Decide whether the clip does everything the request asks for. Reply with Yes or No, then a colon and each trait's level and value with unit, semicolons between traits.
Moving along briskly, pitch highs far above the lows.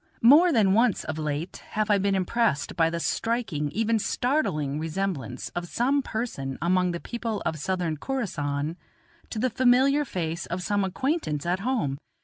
No: average, 160 wpm; wide, 6.8 semitones